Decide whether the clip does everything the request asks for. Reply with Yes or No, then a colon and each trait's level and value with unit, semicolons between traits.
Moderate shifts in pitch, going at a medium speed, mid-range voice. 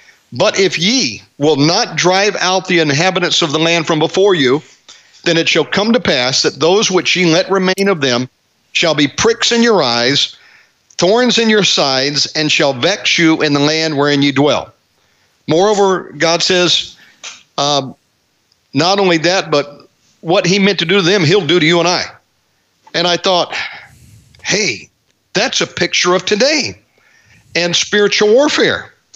Yes: average, 5.0 semitones; average, 170 wpm; medium, 170 Hz